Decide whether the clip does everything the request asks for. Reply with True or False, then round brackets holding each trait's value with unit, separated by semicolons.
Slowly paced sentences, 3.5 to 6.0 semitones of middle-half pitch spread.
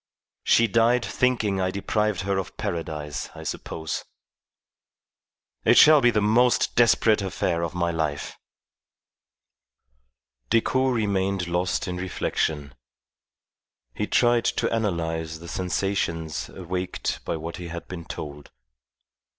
True (120 wpm; 4.6 semitones)